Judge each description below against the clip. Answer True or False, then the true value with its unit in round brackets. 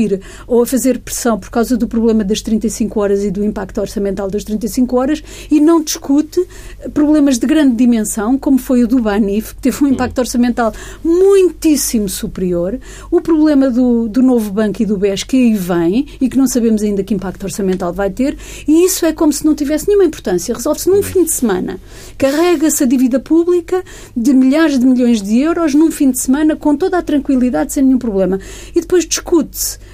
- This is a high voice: True (255 Hz)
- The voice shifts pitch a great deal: True (5.8 semitones)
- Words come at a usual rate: False (195 wpm)